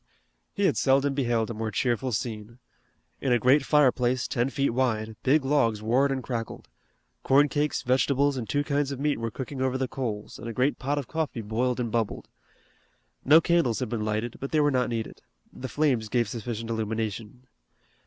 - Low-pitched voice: Yes, low, 125 Hz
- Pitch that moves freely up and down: No, average, 3.4 semitones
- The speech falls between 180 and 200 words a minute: Yes, average, 190 wpm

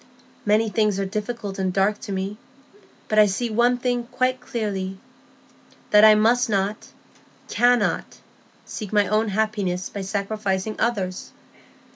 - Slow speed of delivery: Yes, slow, 130 wpm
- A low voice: No, high, 210 Hz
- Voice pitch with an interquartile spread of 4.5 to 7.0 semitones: No, narrow, 2.5 semitones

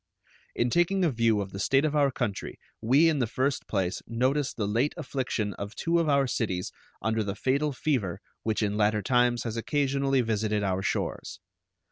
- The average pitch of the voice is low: Yes, low, 120 Hz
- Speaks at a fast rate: No, average, 185 wpm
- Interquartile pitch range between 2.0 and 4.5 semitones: No, average, 4.9 semitones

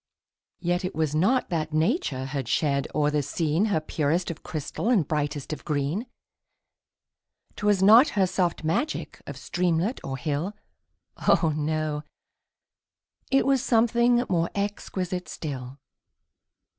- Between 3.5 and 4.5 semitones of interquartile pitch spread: No, average, 5.2 semitones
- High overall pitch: No, medium, 165 Hz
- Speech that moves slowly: Yes, slow, 130 wpm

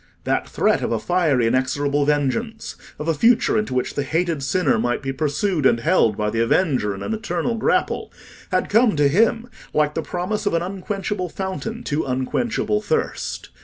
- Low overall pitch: No, medium, 165 Hz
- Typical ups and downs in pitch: No, wide, 7.6 semitones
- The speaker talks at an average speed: Yes, average, 175 wpm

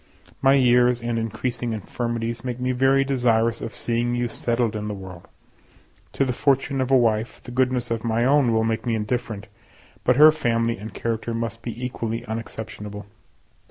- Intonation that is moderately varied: No, narrow, 1.9 semitones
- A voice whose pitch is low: Yes, low, 115 Hz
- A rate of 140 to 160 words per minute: No, average, 175 wpm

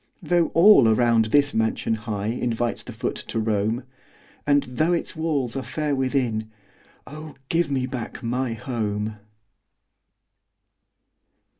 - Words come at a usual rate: No, slow, 125 wpm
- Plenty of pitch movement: No, average, 4.3 semitones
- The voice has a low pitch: Yes, low, 125 Hz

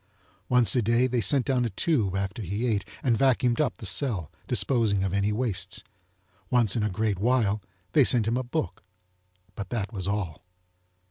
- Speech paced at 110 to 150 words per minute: No, average, 185 wpm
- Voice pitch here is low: Yes, low, 110 Hz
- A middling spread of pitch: Yes, average, 3.8 semitones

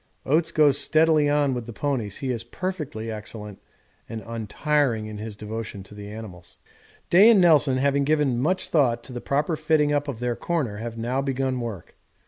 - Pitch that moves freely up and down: No, average, 4.9 semitones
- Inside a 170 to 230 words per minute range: Yes, average, 185 wpm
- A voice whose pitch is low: Yes, low, 130 Hz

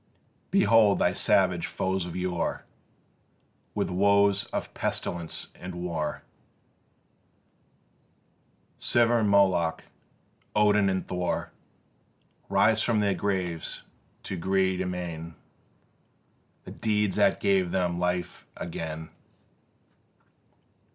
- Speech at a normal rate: No, slow, 90 wpm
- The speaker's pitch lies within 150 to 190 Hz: No, very low, 95 Hz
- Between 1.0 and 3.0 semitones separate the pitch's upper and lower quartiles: Yes, narrow, 2.6 semitones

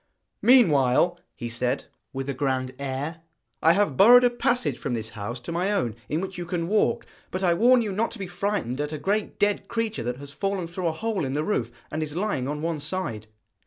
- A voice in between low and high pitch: Yes, medium, 165 Hz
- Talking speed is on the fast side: Yes, fast, 225 wpm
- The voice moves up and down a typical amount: No, wide, 7.0 semitones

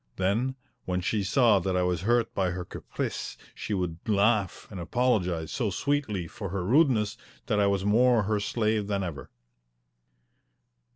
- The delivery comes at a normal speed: Yes, average, 160 wpm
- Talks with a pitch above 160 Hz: No, low, 100 Hz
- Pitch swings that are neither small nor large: Yes, average, 3.8 semitones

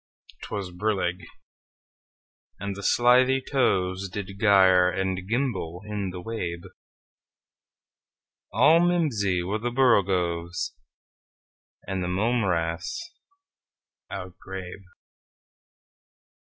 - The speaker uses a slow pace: Yes, slow, 75 wpm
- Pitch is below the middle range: Yes, very low, 95 Hz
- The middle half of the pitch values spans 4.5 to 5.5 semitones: No, average, 4.1 semitones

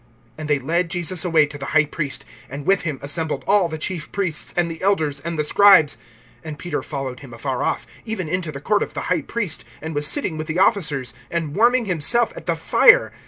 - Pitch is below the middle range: No, medium, 160 Hz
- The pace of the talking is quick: Yes, fast, 220 wpm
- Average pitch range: Yes, average, 4.2 semitones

